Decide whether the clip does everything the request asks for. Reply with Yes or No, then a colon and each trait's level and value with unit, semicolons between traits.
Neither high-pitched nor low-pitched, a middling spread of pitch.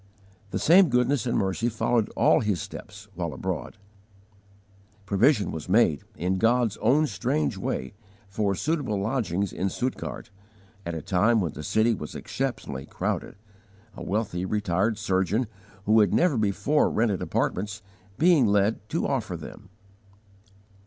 No: low, 105 Hz; average, 4.2 semitones